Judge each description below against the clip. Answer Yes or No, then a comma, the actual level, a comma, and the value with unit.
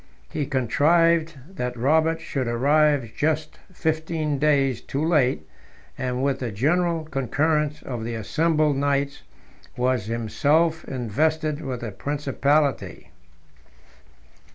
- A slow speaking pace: Yes, slow, 105 wpm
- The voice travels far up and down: No, average, 3.8 semitones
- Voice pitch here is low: No, medium, 145 Hz